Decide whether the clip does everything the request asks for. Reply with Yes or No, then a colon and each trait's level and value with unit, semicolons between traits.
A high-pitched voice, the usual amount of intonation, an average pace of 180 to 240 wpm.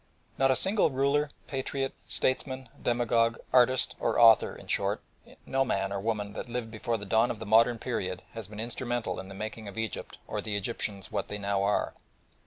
No: low, 115 Hz; average, 3.5 semitones; average, 195 wpm